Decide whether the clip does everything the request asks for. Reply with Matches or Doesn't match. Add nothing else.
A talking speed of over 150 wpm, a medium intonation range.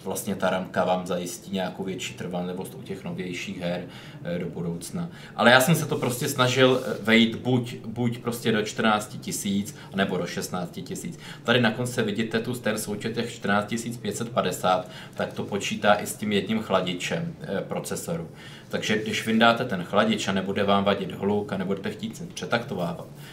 Matches